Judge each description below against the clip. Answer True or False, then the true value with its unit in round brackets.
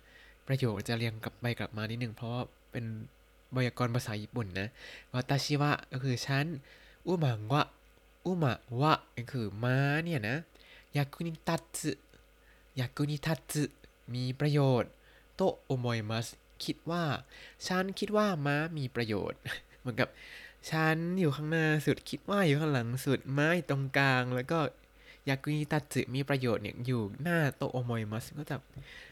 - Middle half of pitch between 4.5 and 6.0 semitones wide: False (3.8 semitones)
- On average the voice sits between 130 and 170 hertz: True (135 Hz)